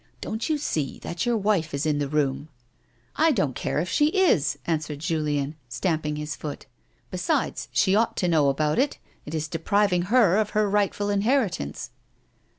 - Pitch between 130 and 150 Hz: No, medium, 165 Hz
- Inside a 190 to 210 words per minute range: Yes, average, 200 wpm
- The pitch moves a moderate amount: No, wide, 5.8 semitones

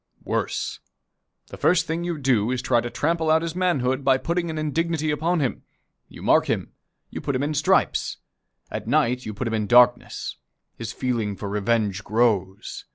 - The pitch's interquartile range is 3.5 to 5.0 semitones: No, wide, 5.6 semitones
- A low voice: Yes, low, 130 Hz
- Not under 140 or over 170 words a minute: No, average, 185 wpm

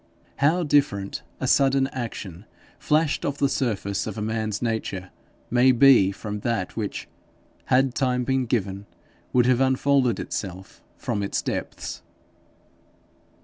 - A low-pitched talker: Yes, low, 120 Hz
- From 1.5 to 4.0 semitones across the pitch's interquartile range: No, average, 4.7 semitones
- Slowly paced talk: Yes, slow, 130 wpm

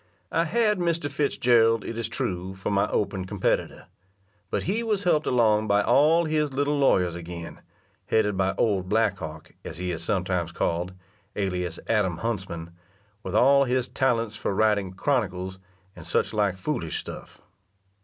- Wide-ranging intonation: Yes, wide, 6.5 semitones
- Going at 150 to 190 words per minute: Yes, average, 155 wpm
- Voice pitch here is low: Yes, low, 105 Hz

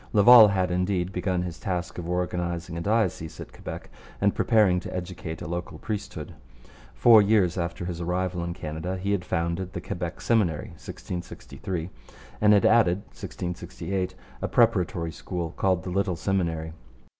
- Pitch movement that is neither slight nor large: No, narrow, 2.3 semitones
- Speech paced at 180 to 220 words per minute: No, average, 155 wpm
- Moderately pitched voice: No, very low, 90 Hz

